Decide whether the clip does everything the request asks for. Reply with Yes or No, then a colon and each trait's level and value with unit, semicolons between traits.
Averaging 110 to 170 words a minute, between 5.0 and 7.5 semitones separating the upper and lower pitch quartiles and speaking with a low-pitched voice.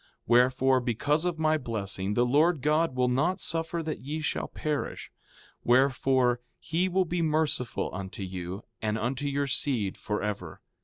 Yes: average, 155 wpm; wide, 5.4 semitones; low, 130 Hz